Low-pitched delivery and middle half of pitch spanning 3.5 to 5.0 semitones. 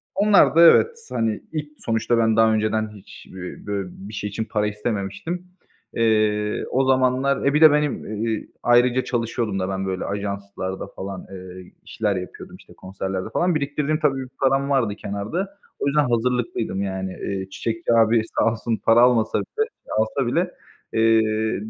Yes: low, 115 Hz; average, 4.7 semitones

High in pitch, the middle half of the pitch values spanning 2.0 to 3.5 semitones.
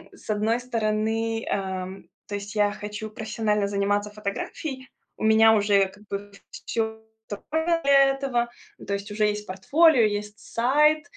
Yes: high, 215 Hz; narrow, 2.6 semitones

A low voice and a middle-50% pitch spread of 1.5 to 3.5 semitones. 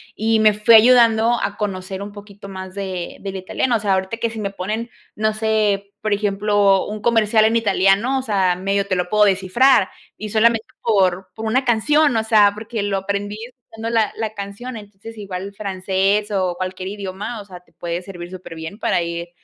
No: high, 205 Hz; narrow, 2.6 semitones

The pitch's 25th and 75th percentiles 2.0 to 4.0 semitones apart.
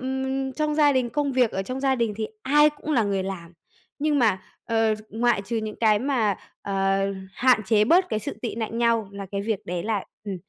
No: average, 4.4 semitones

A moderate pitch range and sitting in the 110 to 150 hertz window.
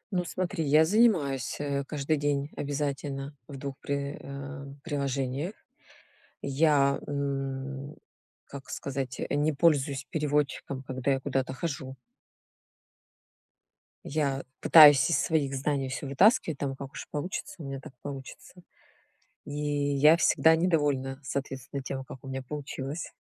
No: narrow, 1.7 semitones; medium, 140 Hz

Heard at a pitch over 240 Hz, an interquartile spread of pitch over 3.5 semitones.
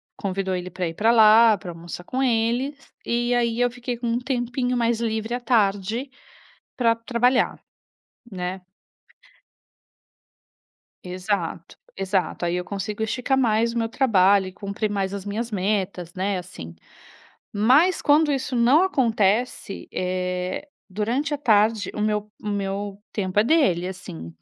No: high, 215 Hz; average, 4.2 semitones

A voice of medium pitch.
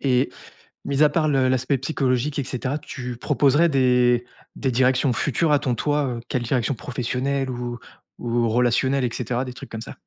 No: low, 130 Hz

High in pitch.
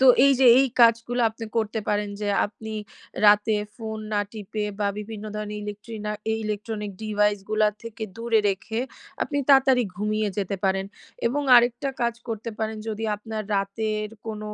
Yes: high, 215 Hz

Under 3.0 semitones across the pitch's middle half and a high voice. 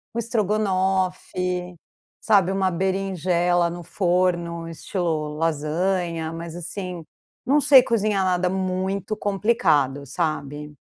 No: narrow, 2.5 semitones; medium, 180 Hz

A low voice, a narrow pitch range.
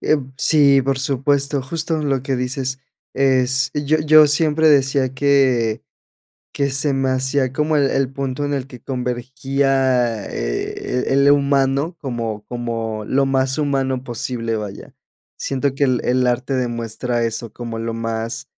Yes: low, 130 Hz; narrow, 2.3 semitones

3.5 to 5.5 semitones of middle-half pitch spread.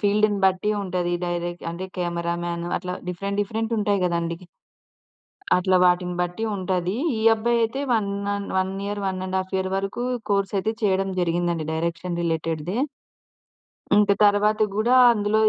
No: average, 2.9 semitones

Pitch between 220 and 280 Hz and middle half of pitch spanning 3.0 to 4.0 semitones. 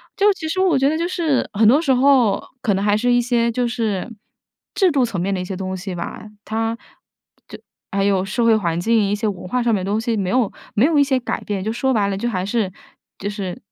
No: high, 225 Hz; average, 4.5 semitones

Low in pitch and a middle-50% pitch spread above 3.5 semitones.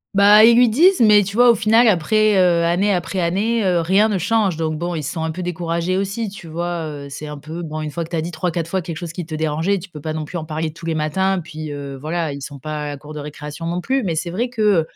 No: medium, 170 Hz; average, 4.1 semitones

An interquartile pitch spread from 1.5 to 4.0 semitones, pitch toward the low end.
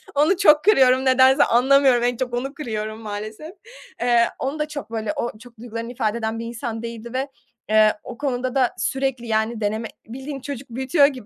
No: average, 2.9 semitones; high, 245 Hz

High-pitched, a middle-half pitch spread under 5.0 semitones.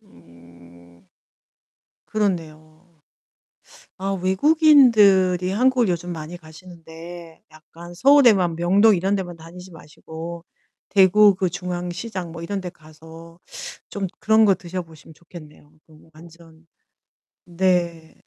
No: medium, 175 Hz; average, 2.9 semitones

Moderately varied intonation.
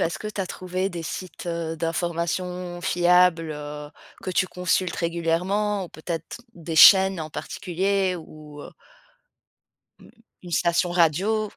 No: narrow, 2.0 semitones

